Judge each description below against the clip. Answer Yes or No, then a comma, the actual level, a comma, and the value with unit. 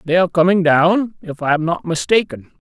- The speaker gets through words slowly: No, fast, 205 wpm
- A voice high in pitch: No, medium, 165 Hz